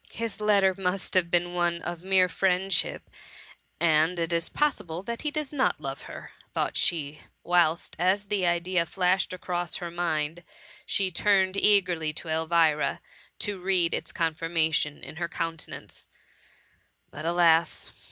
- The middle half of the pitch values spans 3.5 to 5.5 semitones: No, narrow, 2.5 semitones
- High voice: No, medium, 175 Hz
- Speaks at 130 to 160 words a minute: Yes, average, 150 wpm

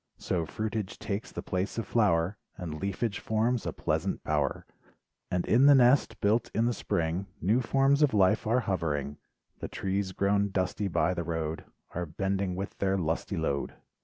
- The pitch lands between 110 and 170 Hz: No, low, 100 Hz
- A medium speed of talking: Yes, average, 170 wpm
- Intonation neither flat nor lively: Yes, average, 4.5 semitones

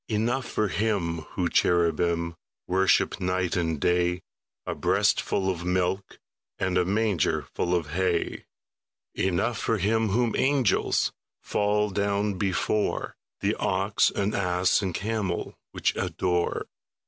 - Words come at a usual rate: No, slow, 120 wpm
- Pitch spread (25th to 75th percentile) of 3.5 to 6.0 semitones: No, average, 2.9 semitones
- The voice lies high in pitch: No, very low, 95 Hz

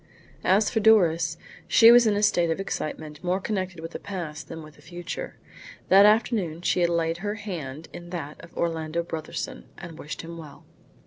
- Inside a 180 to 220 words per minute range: Yes, average, 190 wpm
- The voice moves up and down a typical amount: Yes, average, 3.8 semitones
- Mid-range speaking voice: Yes, medium, 170 Hz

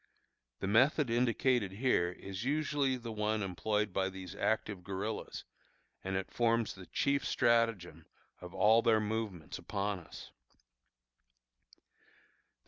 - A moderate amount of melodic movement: Yes, average, 3.6 semitones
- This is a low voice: Yes, low, 110 Hz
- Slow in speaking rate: Yes, slow, 120 wpm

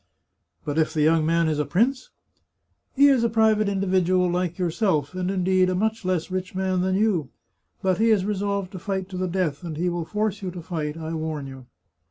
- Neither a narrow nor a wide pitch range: Yes, average, 3.3 semitones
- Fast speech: Yes, fast, 230 wpm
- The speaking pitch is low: No, medium, 185 Hz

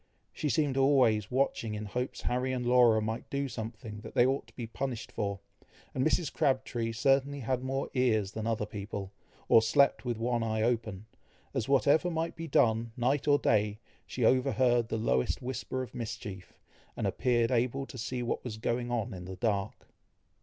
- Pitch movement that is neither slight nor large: Yes, average, 3.0 semitones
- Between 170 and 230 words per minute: Yes, average, 180 wpm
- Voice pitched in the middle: No, low, 120 Hz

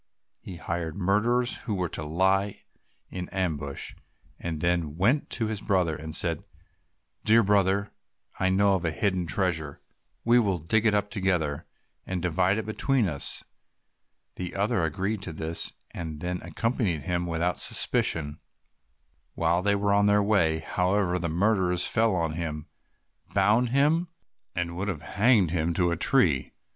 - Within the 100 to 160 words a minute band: Yes, average, 155 wpm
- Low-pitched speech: Yes, very low, 90 Hz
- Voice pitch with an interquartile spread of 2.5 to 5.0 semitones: Yes, average, 3.6 semitones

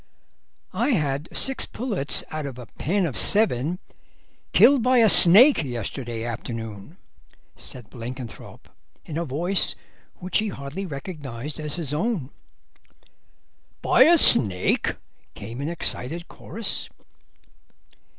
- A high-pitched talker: No, medium, 150 Hz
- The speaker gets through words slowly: Yes, slow, 115 wpm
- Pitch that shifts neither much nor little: No, wide, 7.5 semitones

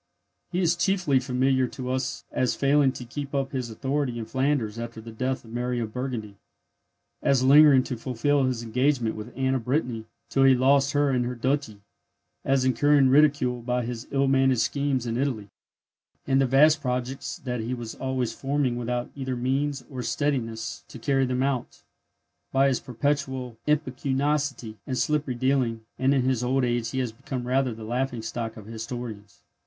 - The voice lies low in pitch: Yes, low, 130 Hz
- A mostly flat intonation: Yes, narrow, 2.3 semitones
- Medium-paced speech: Yes, average, 180 wpm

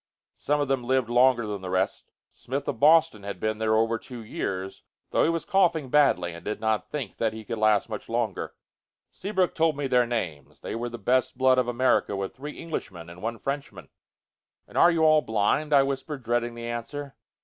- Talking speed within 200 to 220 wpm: Yes, fast, 205 wpm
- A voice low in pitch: Yes, low, 120 Hz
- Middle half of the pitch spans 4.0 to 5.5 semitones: Yes, average, 4.7 semitones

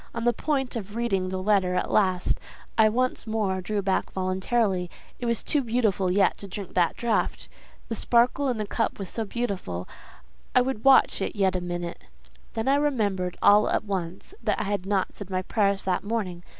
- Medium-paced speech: Yes, average, 190 wpm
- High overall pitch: Yes, high, 205 Hz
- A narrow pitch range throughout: No, average, 3.8 semitones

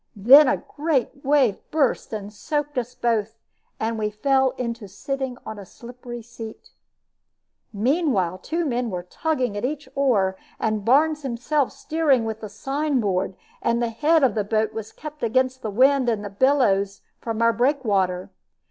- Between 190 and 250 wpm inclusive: No, average, 165 wpm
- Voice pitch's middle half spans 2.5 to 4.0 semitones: No, average, 4.4 semitones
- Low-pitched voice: No, high, 240 Hz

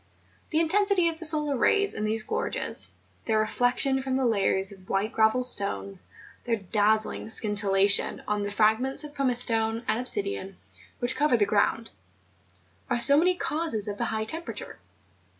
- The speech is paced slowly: No, average, 160 wpm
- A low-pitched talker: No, high, 230 Hz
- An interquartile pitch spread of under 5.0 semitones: No, wide, 5.6 semitones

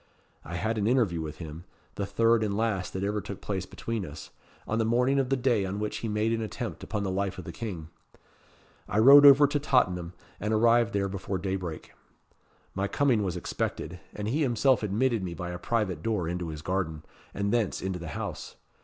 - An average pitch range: Yes, average, 4.2 semitones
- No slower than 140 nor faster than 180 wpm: No, fast, 205 wpm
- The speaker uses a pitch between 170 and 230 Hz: No, low, 100 Hz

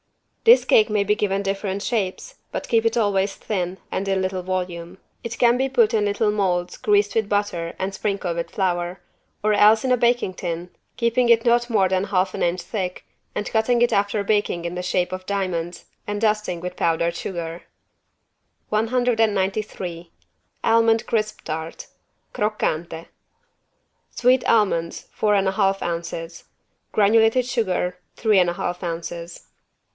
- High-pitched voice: Yes, high, 200 Hz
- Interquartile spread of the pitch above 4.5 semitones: No, average, 3.6 semitones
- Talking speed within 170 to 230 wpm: No, average, 160 wpm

